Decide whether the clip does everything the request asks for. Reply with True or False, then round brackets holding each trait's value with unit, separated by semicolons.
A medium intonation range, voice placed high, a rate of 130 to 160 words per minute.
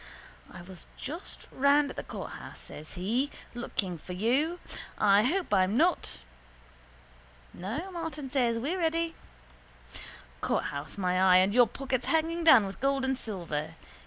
False (8.3 semitones; 240 Hz; 140 wpm)